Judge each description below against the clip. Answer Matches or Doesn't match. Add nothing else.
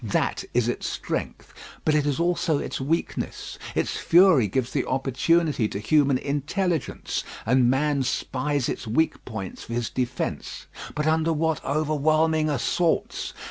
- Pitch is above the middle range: Doesn't match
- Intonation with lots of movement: Doesn't match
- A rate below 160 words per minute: Matches